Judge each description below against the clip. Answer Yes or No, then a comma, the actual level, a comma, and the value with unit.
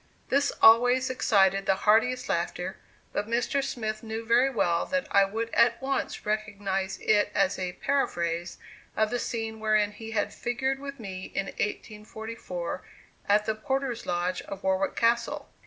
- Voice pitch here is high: Yes, high, 220 Hz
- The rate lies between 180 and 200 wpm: No, average, 155 wpm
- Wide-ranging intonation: No, average, 3.6 semitones